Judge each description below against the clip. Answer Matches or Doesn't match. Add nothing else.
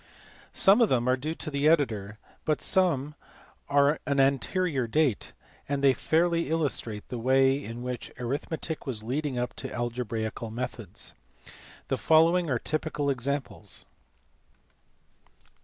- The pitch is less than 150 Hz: Matches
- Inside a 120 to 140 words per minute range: Matches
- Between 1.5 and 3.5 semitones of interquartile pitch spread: Doesn't match